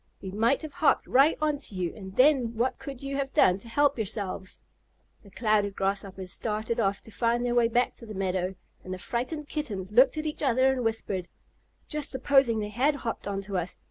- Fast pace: Yes, fast, 210 wpm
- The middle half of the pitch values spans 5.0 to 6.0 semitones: Yes, wide, 5.5 semitones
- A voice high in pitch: Yes, high, 230 Hz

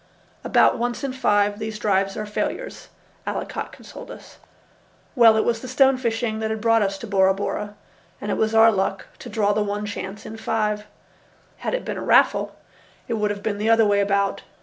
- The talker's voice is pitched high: Yes, high, 215 Hz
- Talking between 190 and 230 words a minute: Yes, average, 200 wpm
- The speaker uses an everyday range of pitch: No, narrow, 1.8 semitones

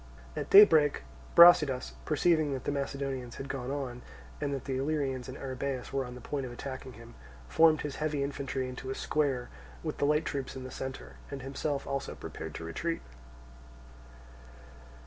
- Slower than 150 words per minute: No, average, 170 wpm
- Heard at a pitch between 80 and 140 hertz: Yes, low, 135 Hz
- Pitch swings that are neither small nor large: No, narrow, 2.2 semitones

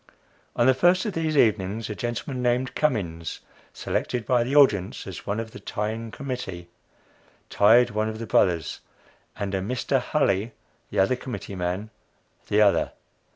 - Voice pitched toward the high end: No, low, 110 Hz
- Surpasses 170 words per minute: No, average, 155 wpm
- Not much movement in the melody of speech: No, average, 4.2 semitones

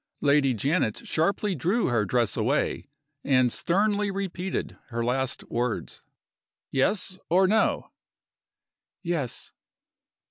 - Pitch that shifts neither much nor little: No, wide, 7.5 semitones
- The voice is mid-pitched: Yes, medium, 150 Hz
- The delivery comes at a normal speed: No, slow, 100 wpm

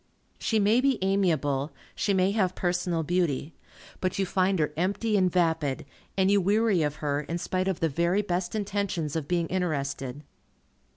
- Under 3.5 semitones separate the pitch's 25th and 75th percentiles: No, average, 3.8 semitones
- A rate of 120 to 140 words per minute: No, average, 170 wpm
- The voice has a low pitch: No, medium, 180 Hz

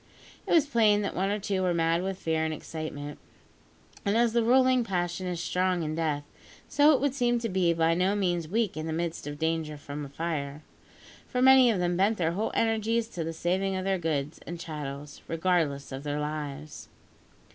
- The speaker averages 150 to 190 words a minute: No, average, 200 wpm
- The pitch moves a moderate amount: Yes, average, 4.8 semitones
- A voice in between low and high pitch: Yes, medium, 175 Hz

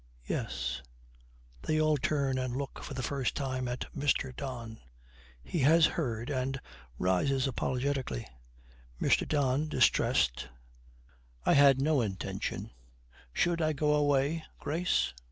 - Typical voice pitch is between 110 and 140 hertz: Yes, low, 135 Hz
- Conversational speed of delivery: No, slow, 120 wpm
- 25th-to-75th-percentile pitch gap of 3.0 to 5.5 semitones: No, narrow, 2.6 semitones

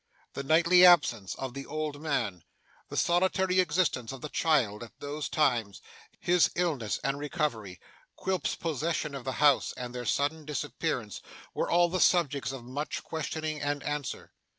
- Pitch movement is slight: No, average, 4.2 semitones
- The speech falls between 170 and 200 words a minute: No, average, 155 wpm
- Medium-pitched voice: Yes, medium, 145 Hz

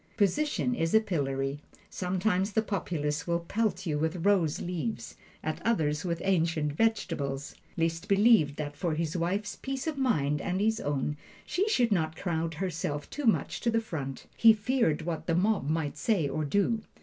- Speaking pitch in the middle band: Yes, medium, 175 Hz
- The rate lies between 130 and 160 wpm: No, average, 175 wpm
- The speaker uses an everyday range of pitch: No, wide, 5.9 semitones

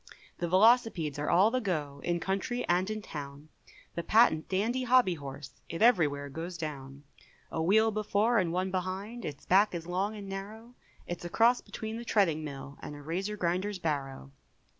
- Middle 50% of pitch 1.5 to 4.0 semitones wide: No, wide, 5.6 semitones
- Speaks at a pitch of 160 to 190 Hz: Yes, medium, 185 Hz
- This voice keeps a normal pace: Yes, average, 180 wpm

